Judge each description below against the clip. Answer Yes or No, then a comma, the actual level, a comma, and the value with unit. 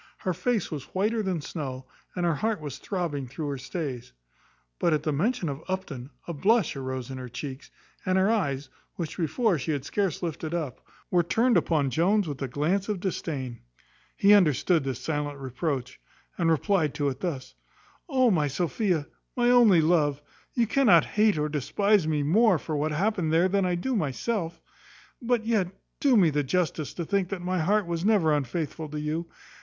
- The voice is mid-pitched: Yes, medium, 165 Hz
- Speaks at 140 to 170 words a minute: No, average, 185 wpm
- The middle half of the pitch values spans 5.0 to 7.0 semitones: Yes, average, 5.3 semitones